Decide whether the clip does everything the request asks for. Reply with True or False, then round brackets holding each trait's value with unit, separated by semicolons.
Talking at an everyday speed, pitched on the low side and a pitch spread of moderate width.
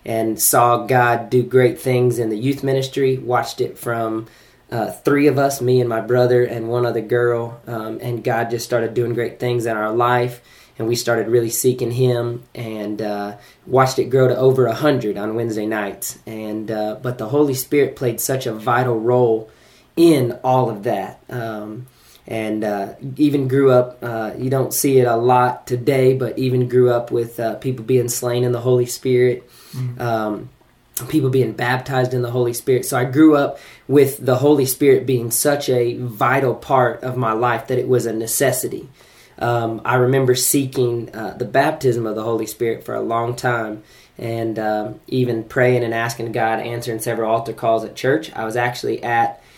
False (190 wpm; 120 Hz; 2.0 semitones)